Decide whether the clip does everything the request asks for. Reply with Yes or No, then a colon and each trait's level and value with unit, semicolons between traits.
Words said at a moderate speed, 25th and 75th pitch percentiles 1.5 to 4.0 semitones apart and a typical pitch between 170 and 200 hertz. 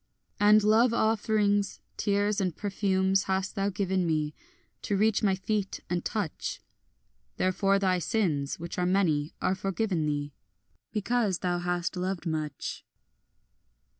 No: slow, 130 wpm; average, 2.7 semitones; high, 190 Hz